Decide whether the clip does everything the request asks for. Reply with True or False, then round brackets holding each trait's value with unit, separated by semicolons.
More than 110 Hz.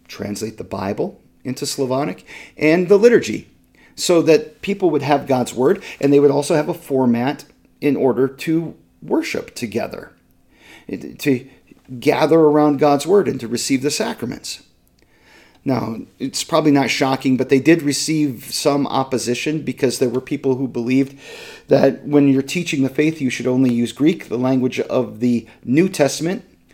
True (140 Hz)